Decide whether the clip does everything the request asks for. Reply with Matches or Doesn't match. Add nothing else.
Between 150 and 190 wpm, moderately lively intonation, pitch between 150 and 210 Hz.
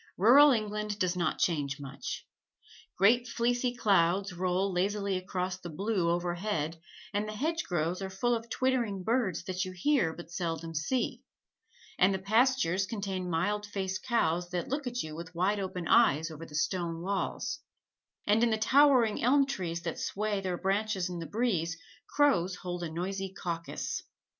Matches